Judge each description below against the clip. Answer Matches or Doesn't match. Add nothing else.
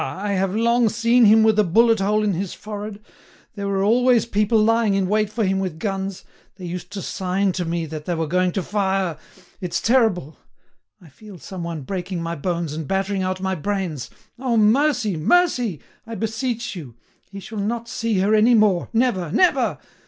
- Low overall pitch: Doesn't match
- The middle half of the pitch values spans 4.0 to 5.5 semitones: Doesn't match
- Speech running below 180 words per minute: Doesn't match